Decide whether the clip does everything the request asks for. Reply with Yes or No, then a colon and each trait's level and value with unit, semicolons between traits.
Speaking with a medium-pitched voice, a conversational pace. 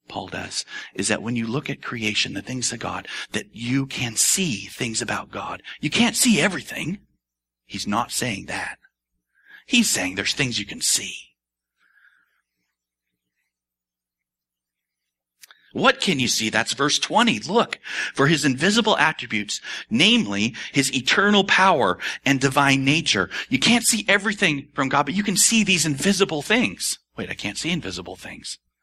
No: low, 125 Hz; average, 150 wpm